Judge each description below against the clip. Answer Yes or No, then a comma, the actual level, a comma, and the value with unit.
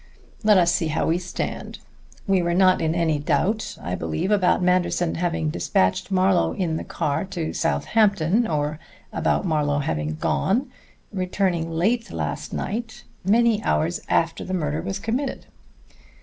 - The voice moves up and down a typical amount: Yes, average, 3.8 semitones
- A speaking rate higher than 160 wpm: No, average, 150 wpm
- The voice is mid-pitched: Yes, medium, 175 Hz